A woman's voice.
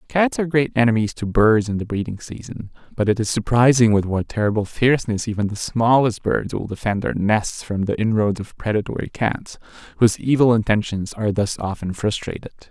No: male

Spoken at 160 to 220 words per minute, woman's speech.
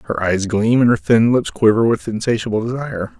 No: fast, 205 wpm; male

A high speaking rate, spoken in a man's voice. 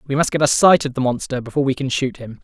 Yes: fast, 320 wpm; male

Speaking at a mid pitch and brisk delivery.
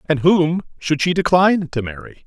No: medium, 160 Hz; average, 185 wpm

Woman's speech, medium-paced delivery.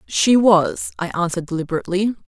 No: female; slow, 130 wpm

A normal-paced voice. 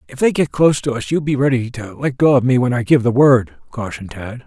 No: fast, 280 wpm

